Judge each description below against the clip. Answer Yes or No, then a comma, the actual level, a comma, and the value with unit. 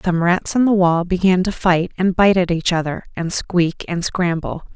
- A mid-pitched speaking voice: Yes, medium, 180 Hz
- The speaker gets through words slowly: No, average, 200 wpm